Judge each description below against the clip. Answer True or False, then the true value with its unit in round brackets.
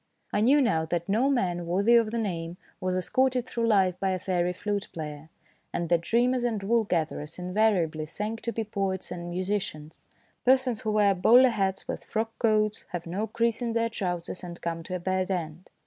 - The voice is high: True (195 Hz)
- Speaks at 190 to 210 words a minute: True (195 wpm)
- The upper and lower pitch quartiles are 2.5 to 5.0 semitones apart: True (4.5 semitones)